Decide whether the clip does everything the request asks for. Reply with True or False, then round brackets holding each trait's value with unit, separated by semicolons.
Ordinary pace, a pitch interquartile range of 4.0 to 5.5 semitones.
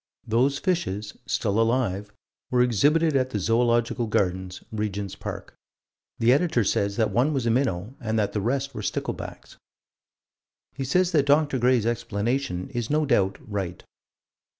True (150 wpm; 4.8 semitones)